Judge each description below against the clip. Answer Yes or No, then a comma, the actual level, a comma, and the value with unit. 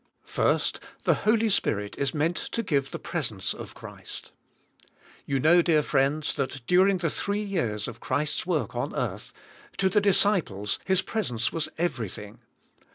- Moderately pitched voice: Yes, medium, 155 Hz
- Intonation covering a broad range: Yes, wide, 6.4 semitones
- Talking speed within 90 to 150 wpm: No, average, 160 wpm